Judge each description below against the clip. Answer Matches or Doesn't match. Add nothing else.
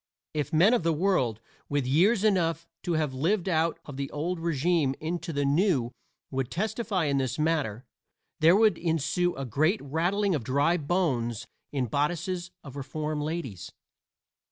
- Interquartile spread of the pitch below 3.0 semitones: Doesn't match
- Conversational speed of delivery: Matches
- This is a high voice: Doesn't match